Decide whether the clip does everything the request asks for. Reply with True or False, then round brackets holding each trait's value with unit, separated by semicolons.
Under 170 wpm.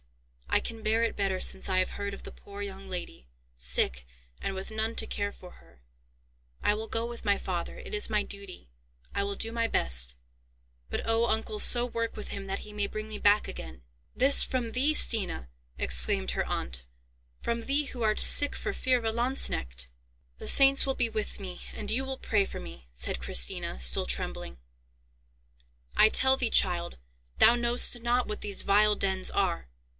False (190 wpm)